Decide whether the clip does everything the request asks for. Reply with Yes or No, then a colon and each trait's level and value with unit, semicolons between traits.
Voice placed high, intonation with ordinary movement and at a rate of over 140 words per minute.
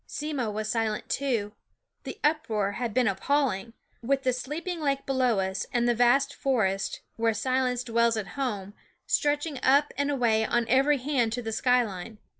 Yes: high, 245 Hz; average, 3.9 semitones; average, 170 wpm